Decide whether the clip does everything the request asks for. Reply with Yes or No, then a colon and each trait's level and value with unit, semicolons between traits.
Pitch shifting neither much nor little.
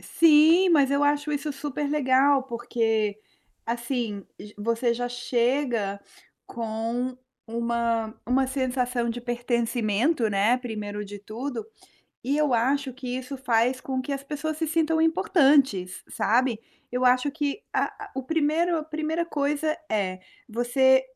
Yes: average, 3.7 semitones